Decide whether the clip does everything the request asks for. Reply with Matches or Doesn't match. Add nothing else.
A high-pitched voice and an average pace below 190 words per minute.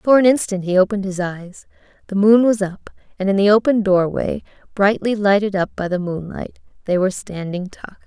Doesn't match